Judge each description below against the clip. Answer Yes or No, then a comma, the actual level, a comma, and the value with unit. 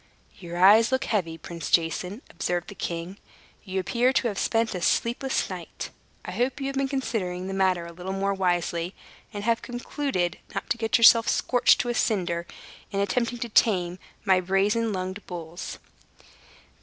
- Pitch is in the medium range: No, high, 195 Hz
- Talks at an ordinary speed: Yes, average, 170 wpm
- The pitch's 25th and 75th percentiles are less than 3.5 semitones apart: No, average, 4.6 semitones